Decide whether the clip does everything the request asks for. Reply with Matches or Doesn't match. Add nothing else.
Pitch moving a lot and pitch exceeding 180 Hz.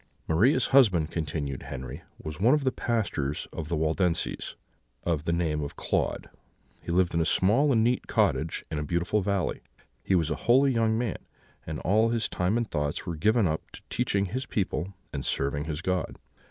Doesn't match